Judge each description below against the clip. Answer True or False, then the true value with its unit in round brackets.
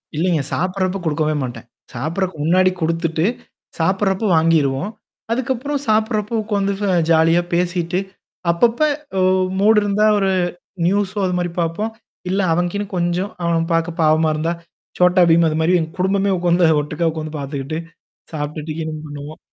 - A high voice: False (170 Hz)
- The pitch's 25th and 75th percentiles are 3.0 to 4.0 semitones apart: True (3.5 semitones)